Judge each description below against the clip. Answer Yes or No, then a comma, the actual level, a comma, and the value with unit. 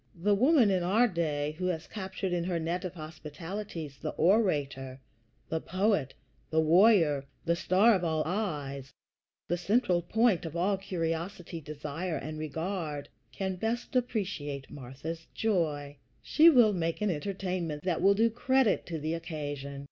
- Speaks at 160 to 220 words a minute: No, average, 150 wpm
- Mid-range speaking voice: Yes, medium, 170 Hz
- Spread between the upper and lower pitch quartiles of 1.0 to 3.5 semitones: No, average, 4.4 semitones